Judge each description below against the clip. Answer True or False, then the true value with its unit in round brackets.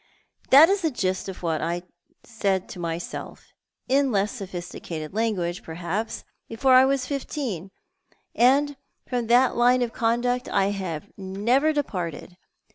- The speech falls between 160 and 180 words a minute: False (135 wpm)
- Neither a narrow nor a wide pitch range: False (6.0 semitones)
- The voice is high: True (220 Hz)